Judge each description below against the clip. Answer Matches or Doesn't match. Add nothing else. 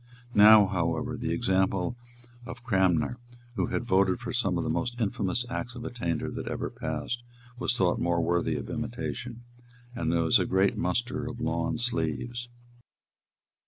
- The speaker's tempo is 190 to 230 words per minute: Doesn't match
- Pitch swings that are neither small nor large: Doesn't match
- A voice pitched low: Matches